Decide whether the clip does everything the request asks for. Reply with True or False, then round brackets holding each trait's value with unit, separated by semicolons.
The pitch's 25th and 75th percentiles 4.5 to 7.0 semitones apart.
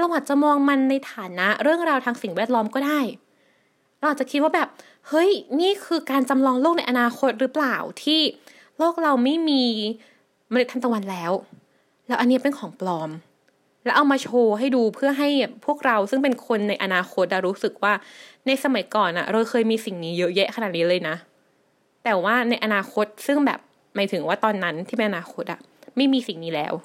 True (5.3 semitones)